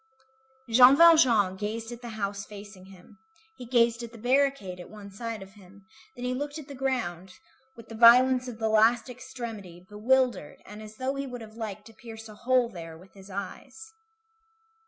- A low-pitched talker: No, high, 225 Hz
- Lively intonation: No, average, 3.8 semitones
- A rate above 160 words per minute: Yes, average, 190 wpm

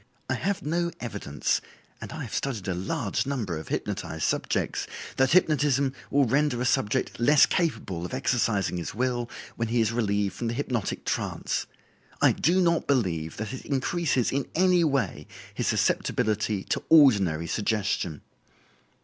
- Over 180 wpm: No, average, 155 wpm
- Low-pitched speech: Yes, low, 120 Hz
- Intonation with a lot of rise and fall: Yes, wide, 5.7 semitones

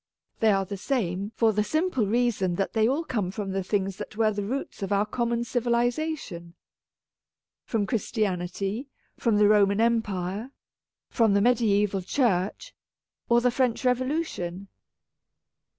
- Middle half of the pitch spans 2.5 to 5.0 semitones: Yes, average, 3.6 semitones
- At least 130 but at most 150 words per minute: Yes, average, 145 wpm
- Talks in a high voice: Yes, high, 215 Hz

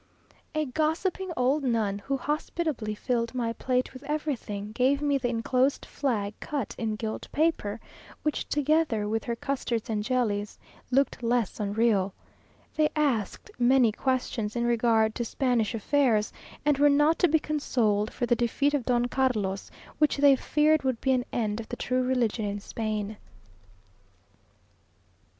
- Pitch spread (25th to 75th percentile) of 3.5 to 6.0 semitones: Yes, average, 4.4 semitones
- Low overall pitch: No, high, 245 Hz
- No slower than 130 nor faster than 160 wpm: Yes, average, 150 wpm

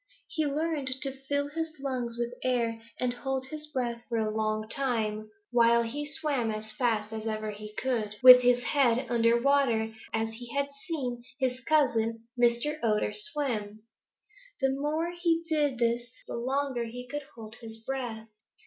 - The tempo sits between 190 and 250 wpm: No, average, 165 wpm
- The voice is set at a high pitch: Yes, high, 245 Hz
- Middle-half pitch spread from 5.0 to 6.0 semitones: No, average, 3.7 semitones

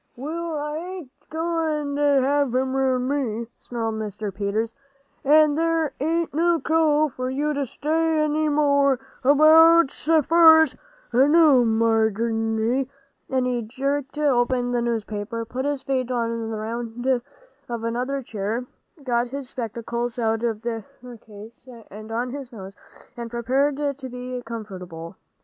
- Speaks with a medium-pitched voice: No, very high, 255 Hz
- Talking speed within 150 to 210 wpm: No, average, 140 wpm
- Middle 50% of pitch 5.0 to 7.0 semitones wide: No, average, 4.2 semitones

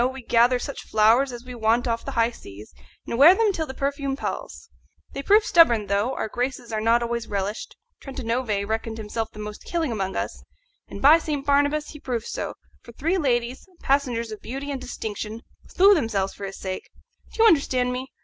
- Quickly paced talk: No, average, 195 wpm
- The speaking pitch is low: No, high, 245 Hz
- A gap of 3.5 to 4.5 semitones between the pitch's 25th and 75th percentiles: Yes, average, 4.2 semitones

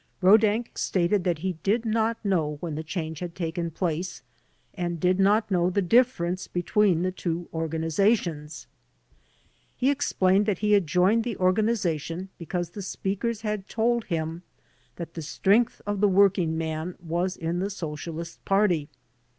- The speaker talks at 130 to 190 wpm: Yes, average, 150 wpm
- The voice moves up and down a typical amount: Yes, average, 3.7 semitones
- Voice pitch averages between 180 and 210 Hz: Yes, medium, 185 Hz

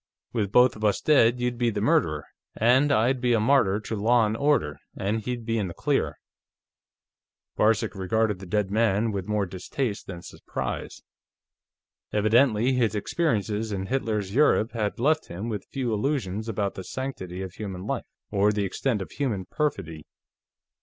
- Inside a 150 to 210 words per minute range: Yes, average, 165 wpm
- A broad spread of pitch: No, average, 3.7 semitones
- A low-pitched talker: Yes, low, 110 Hz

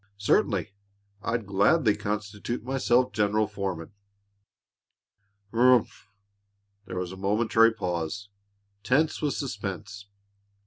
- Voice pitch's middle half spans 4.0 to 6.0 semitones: No, average, 3.0 semitones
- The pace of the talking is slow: Yes, slow, 90 wpm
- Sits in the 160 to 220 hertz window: No, low, 105 Hz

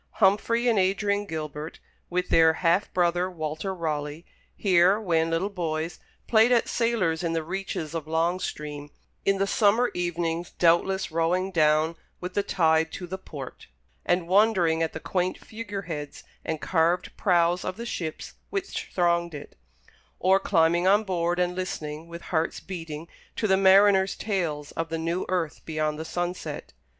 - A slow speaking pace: No, average, 160 wpm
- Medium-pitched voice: Yes, medium, 175 Hz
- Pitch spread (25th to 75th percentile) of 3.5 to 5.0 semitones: No, average, 2.9 semitones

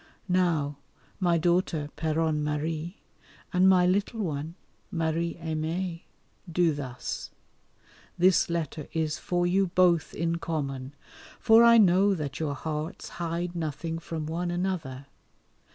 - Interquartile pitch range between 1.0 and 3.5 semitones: Yes, narrow, 2.6 semitones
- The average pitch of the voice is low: No, medium, 165 Hz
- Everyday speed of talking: No, slow, 120 wpm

